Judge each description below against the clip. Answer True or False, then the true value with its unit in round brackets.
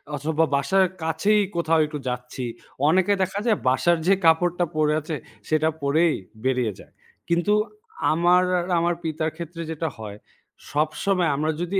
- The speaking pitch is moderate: True (160 Hz)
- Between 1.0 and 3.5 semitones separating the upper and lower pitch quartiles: True (2.7 semitones)